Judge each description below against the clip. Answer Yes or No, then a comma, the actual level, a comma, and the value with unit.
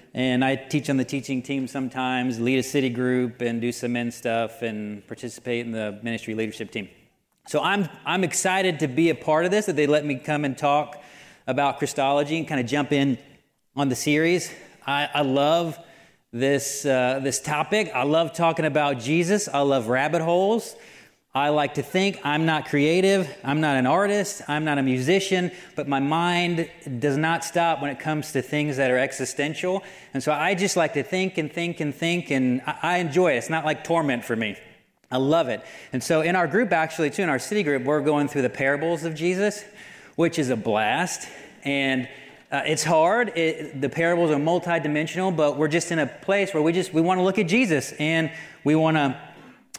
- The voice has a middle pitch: Yes, medium, 150 Hz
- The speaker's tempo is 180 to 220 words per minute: Yes, fast, 205 wpm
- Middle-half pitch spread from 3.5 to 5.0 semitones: Yes, average, 3.8 semitones